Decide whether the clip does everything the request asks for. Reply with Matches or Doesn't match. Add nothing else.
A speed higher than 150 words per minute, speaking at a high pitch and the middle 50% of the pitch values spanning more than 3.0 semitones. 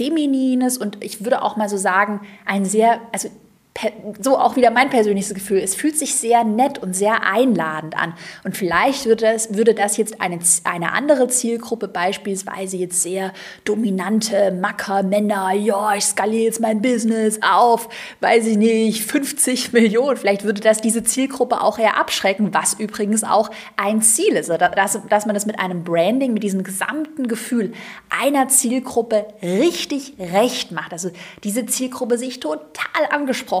Matches